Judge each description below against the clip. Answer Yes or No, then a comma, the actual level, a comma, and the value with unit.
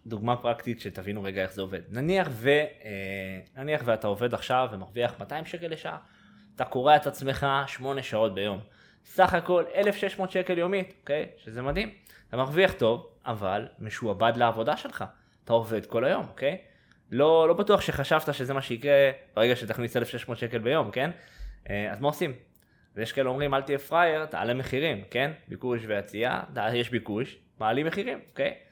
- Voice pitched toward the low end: Yes, low, 130 Hz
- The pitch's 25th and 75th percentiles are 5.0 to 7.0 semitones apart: Yes, average, 5.3 semitones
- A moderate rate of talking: No, fast, 170 wpm